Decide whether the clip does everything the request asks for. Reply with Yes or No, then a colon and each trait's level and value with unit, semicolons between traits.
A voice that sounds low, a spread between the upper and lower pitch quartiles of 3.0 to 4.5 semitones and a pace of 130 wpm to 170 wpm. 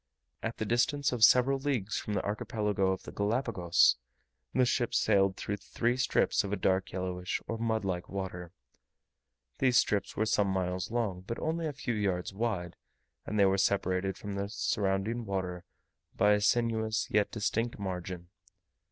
Yes: low, 105 Hz; average, 3.6 semitones; average, 165 wpm